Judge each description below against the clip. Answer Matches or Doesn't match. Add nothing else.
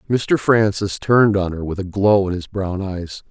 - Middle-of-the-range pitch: Doesn't match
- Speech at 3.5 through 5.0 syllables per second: Matches